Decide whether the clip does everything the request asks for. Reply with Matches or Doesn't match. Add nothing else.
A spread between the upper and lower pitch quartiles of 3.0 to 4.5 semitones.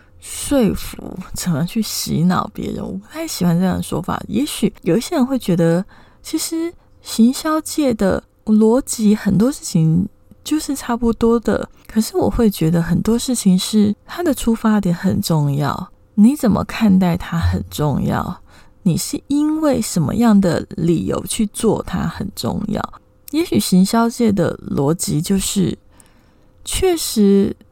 Doesn't match